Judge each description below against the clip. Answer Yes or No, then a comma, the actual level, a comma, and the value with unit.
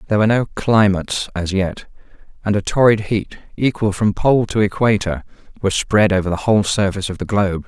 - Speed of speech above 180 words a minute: Yes, average, 190 wpm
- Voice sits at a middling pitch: No, low, 100 Hz